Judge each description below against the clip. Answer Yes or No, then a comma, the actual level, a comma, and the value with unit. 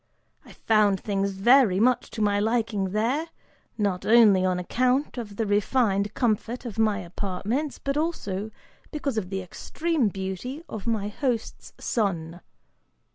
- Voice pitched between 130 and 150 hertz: No, high, 215 Hz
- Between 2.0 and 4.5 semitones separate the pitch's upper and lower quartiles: Yes, average, 4.0 semitones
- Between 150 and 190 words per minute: No, average, 140 wpm